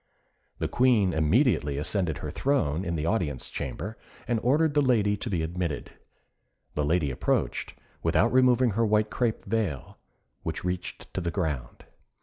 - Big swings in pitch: Yes, wide, 7.0 semitones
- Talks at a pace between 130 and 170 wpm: Yes, average, 150 wpm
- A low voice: Yes, very low, 95 Hz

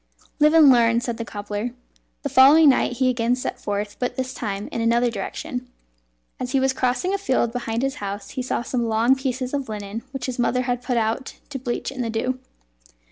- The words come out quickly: Yes, fast, 210 wpm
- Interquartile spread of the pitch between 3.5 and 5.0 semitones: No, narrow, 2.4 semitones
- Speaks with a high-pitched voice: Yes, high, 245 Hz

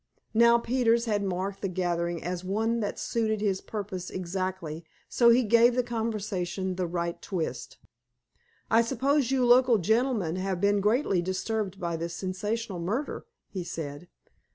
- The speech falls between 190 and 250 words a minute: No, average, 150 wpm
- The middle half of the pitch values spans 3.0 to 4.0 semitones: No, average, 4.4 semitones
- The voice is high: Yes, high, 200 Hz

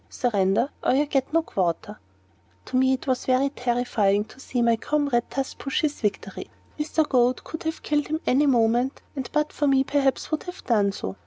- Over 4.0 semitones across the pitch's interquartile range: No, average, 3.7 semitones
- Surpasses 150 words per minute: Yes, average, 200 wpm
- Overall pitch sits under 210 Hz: No, very high, 260 Hz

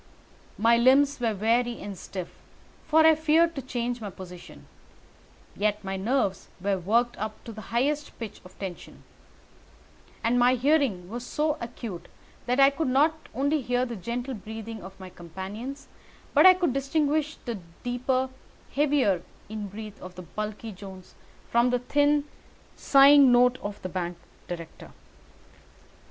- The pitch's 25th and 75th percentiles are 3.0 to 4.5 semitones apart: No, average, 5.3 semitones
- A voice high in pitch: Yes, high, 240 Hz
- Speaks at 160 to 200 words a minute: No, average, 150 wpm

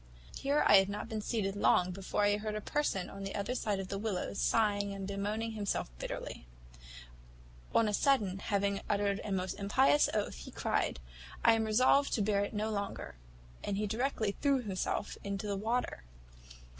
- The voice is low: No, high, 205 Hz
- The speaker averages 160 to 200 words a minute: Yes, average, 180 wpm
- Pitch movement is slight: Yes, narrow, 2.0 semitones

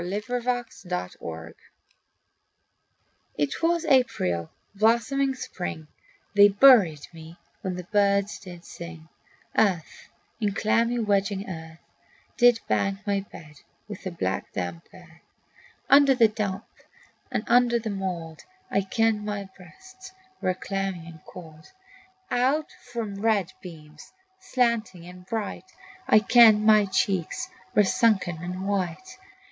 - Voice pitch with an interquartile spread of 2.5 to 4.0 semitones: No, average, 4.7 semitones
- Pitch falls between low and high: No, high, 200 Hz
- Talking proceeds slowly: Yes, slow, 125 wpm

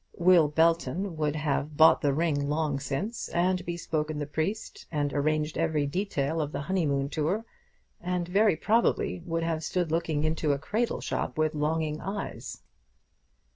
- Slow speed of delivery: No, average, 155 wpm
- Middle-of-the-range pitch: Yes, medium, 160 Hz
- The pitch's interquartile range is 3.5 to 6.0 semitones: No, average, 2.7 semitones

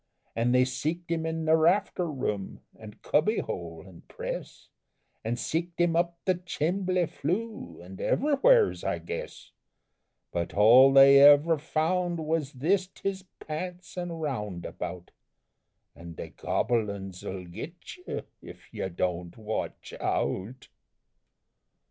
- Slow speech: Yes, slow, 130 wpm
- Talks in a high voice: No, medium, 155 Hz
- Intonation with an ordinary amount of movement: No, wide, 8.9 semitones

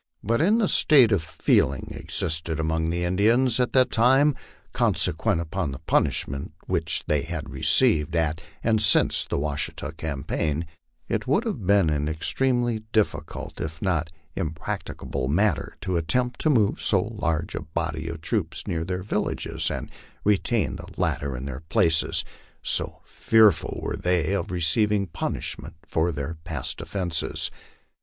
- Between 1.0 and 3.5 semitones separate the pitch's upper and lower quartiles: No, average, 5.2 semitones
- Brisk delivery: No, average, 155 wpm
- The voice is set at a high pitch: No, very low, 85 Hz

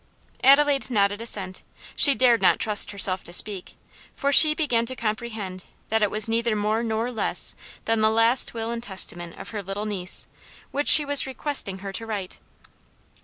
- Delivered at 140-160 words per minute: No, average, 175 wpm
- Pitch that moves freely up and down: No, average, 3.2 semitones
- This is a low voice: No, high, 220 Hz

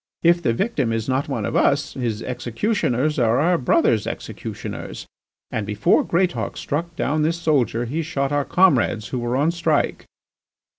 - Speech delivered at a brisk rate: No, average, 160 wpm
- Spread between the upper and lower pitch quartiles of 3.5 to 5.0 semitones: No, wide, 5.6 semitones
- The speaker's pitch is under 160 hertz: Yes, medium, 140 Hz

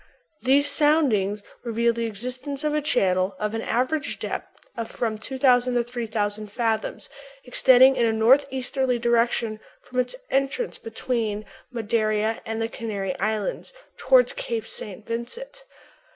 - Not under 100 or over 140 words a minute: Yes, slow, 135 wpm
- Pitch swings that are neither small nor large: Yes, average, 3.6 semitones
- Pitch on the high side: Yes, high, 235 Hz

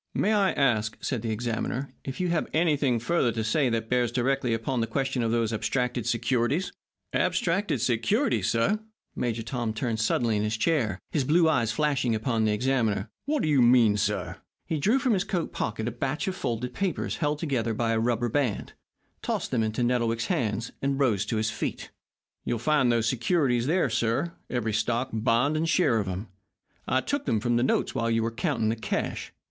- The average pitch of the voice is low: Yes, low, 120 Hz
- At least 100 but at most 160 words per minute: No, average, 195 wpm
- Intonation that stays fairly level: No, average, 4.2 semitones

